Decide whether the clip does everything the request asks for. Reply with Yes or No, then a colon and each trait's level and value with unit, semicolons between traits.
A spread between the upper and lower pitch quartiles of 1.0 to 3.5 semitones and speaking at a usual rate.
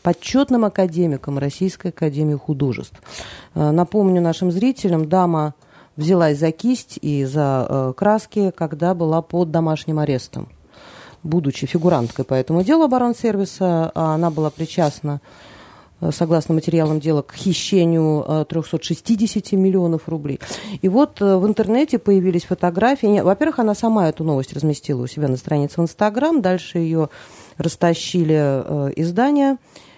No: average, 4.1 semitones; average, 125 wpm